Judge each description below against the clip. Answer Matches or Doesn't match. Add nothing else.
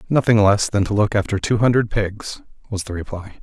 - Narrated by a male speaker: Matches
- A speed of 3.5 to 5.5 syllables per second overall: Matches